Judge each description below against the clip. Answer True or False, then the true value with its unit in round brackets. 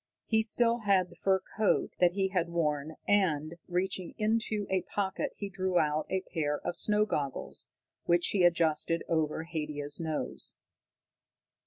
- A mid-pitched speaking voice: True (175 Hz)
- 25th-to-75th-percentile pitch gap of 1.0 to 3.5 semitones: False (3.9 semitones)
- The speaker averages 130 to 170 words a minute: True (150 wpm)